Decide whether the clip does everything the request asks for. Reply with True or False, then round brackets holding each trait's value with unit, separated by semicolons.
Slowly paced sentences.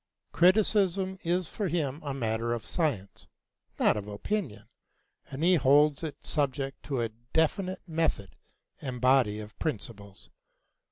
True (130 wpm)